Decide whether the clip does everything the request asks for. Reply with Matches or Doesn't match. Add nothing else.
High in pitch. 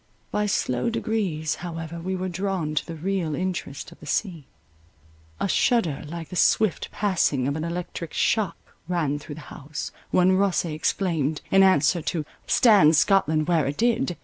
Doesn't match